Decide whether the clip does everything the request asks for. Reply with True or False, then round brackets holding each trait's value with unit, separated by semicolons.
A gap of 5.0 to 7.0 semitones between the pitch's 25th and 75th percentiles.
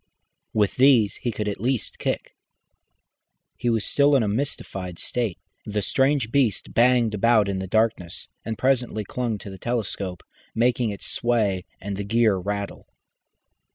False (3.3 semitones)